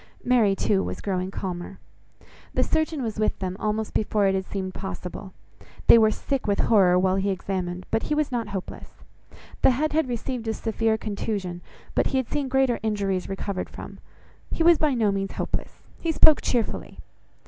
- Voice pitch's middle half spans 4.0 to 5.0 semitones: Yes, average, 4.6 semitones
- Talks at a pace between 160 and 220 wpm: Yes, average, 180 wpm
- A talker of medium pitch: No, high, 210 Hz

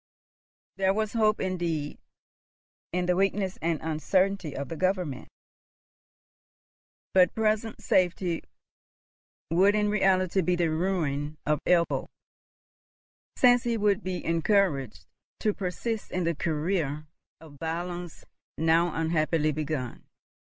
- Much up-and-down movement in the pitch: No, average, 3.6 semitones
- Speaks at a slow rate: Yes, slow, 110 wpm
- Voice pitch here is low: No, medium, 175 Hz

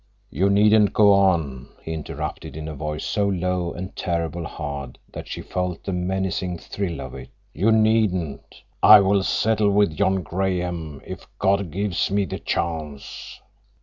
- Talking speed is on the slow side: No, average, 155 wpm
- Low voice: Yes, very low, 90 Hz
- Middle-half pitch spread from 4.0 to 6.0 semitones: No, average, 3.5 semitones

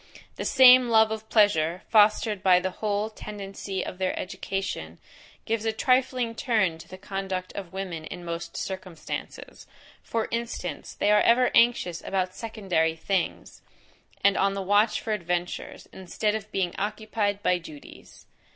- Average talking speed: Yes, average, 150 wpm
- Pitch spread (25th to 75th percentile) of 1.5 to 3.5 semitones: Yes, average, 3.2 semitones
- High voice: Yes, high, 195 Hz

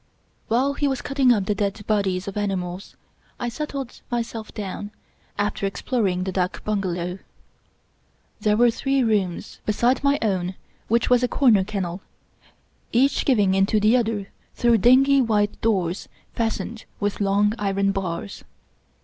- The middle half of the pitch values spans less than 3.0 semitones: No, average, 3.7 semitones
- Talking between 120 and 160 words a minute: Yes, average, 145 wpm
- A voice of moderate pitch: No, high, 210 Hz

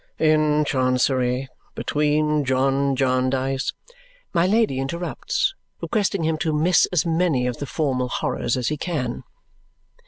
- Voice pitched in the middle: Yes, medium, 145 Hz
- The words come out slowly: Yes, slow, 130 wpm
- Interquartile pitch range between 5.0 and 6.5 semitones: No, average, 4.0 semitones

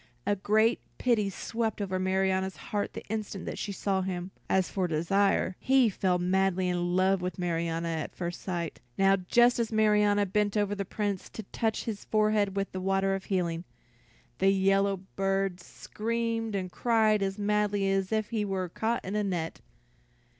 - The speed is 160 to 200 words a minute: Yes, average, 170 wpm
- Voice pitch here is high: Yes, high, 195 Hz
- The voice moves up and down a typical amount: No, narrow, 2.1 semitones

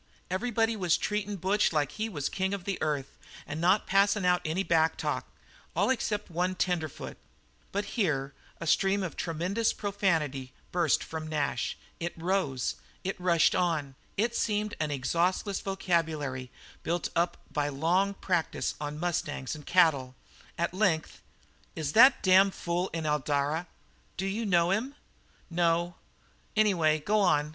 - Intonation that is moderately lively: Yes, average, 4.1 semitones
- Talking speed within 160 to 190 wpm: No, average, 145 wpm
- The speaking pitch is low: No, medium, 175 Hz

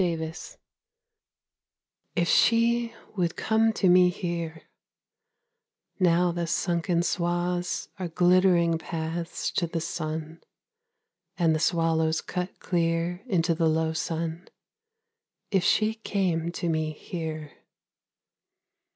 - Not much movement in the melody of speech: Yes, narrow, 1.8 semitones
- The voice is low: No, medium, 170 Hz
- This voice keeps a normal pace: No, slow, 110 wpm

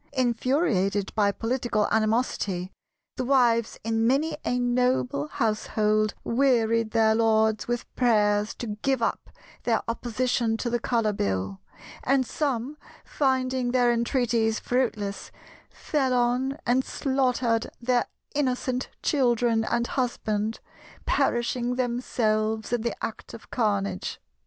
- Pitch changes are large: No, narrow, 2.6 semitones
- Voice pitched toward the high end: Yes, high, 235 Hz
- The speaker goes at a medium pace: No, slow, 115 wpm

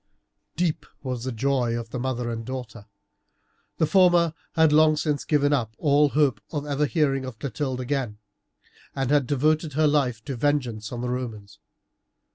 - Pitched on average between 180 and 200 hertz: No, low, 135 Hz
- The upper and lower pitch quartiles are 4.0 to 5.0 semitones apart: No, average, 3.5 semitones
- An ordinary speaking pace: Yes, average, 165 wpm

